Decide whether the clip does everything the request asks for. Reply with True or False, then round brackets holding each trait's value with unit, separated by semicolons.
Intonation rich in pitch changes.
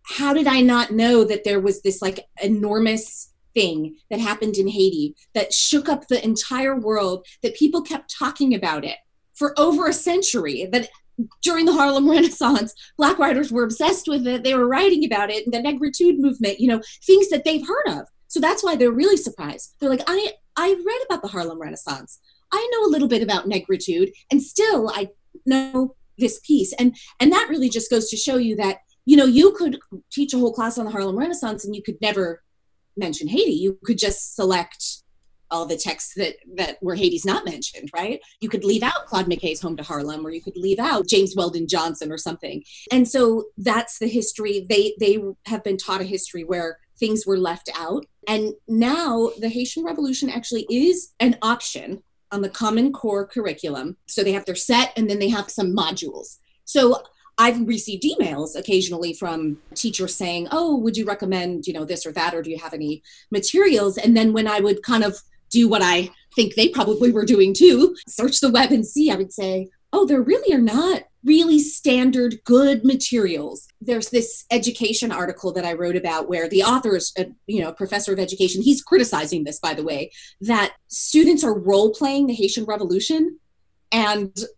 True (6.1 semitones)